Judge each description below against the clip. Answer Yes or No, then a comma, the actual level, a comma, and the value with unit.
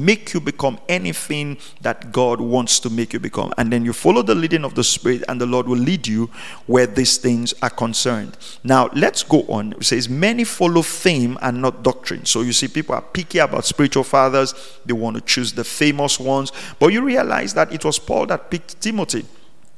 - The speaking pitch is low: Yes, low, 130 Hz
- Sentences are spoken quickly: Yes, fast, 210 wpm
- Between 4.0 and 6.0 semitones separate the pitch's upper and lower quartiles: Yes, average, 4.4 semitones